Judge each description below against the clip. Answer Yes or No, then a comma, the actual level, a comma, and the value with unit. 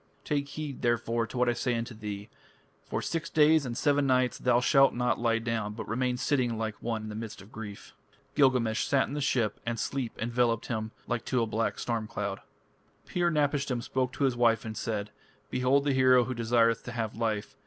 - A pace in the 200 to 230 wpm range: Yes, fast, 205 wpm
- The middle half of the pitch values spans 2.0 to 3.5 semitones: Yes, narrow, 2.6 semitones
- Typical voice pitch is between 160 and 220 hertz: No, low, 120 Hz